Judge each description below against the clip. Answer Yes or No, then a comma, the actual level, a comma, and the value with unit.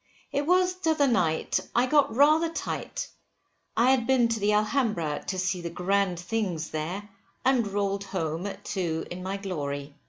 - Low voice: No, high, 200 Hz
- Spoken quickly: No, average, 165 wpm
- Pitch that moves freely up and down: Yes, wide, 6.6 semitones